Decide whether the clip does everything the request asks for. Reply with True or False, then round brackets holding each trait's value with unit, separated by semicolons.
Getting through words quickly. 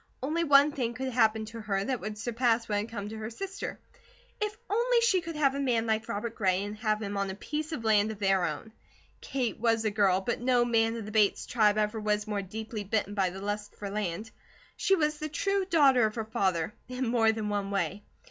True (235 wpm)